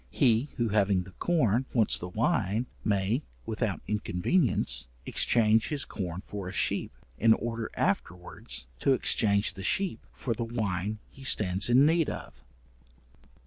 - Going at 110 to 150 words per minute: Yes, average, 145 wpm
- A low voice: Yes, low, 110 Hz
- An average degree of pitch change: Yes, average, 4.2 semitones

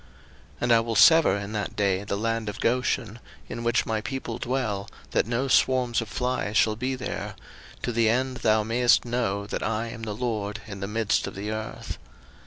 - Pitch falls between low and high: No, low, 115 Hz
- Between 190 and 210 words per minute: Yes, average, 200 wpm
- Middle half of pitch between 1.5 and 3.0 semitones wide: Yes, narrow, 2.6 semitones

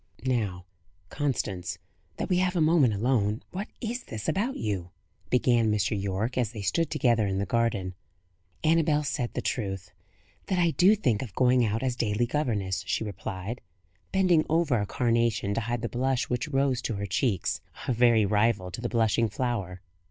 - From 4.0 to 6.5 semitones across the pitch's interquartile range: Yes, average, 4.8 semitones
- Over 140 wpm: Yes, average, 175 wpm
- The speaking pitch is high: No, low, 115 Hz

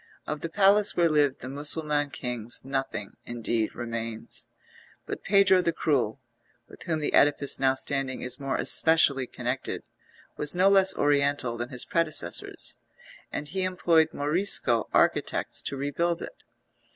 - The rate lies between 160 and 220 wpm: No, average, 140 wpm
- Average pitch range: Yes, average, 4.5 semitones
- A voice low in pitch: No, medium, 145 Hz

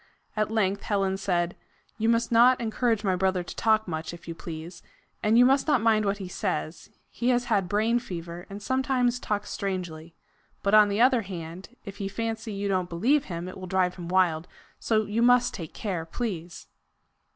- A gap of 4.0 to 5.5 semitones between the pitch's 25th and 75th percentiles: Yes, average, 4.3 semitones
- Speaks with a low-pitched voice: No, high, 200 Hz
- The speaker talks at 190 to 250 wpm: Yes, average, 195 wpm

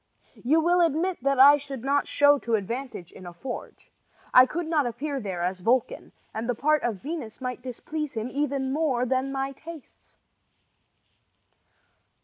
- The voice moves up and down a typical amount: Yes, average, 3.7 semitones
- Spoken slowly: No, average, 160 wpm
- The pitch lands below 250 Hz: No, very high, 270 Hz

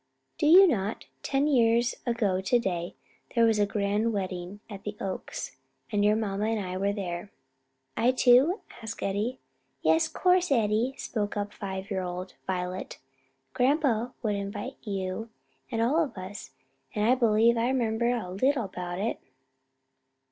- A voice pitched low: No, high, 215 Hz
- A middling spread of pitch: Yes, average, 3.7 semitones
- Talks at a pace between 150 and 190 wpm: Yes, average, 155 wpm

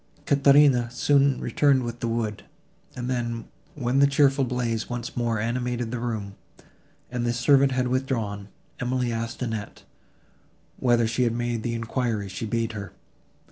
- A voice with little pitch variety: Yes, narrow, 2.0 semitones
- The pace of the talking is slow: No, average, 150 wpm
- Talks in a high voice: No, low, 120 Hz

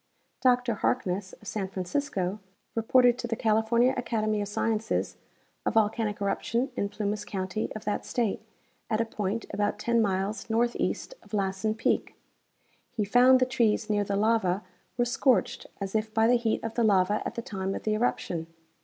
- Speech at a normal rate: Yes, average, 170 wpm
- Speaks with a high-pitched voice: Yes, high, 215 Hz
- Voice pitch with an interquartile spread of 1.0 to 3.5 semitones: Yes, narrow, 2.6 semitones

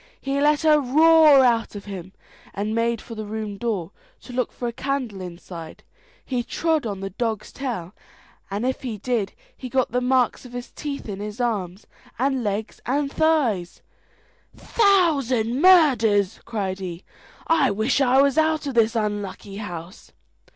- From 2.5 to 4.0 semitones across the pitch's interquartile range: No, average, 5.1 semitones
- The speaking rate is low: No, average, 165 wpm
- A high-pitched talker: Yes, high, 235 Hz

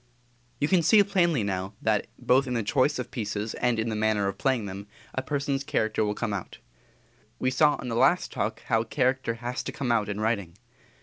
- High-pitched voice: No, low, 115 Hz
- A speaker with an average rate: No, fast, 210 wpm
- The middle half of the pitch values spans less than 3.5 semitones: No, average, 4.2 semitones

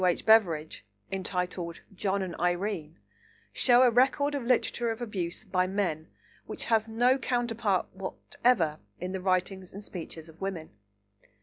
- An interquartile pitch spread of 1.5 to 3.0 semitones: No, average, 4.2 semitones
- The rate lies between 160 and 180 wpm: No, average, 140 wpm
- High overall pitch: Yes, high, 195 Hz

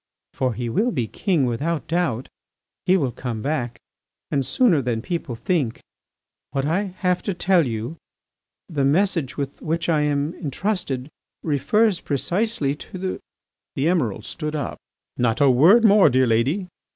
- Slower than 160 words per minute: Yes, average, 150 wpm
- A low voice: No, medium, 150 Hz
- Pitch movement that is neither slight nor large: No, wide, 5.9 semitones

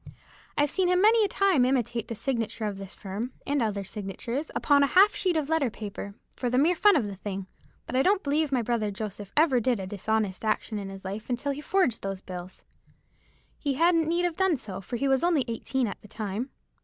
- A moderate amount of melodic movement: No, wide, 6.9 semitones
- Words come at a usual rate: No, fast, 225 wpm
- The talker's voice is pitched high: Yes, high, 245 Hz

